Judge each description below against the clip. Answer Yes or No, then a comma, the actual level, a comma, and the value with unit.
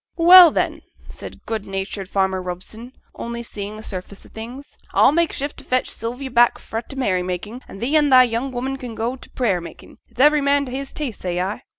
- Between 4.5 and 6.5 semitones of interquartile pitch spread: Yes, average, 5.2 semitones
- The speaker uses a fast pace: Yes, fast, 225 wpm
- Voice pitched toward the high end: Yes, high, 235 Hz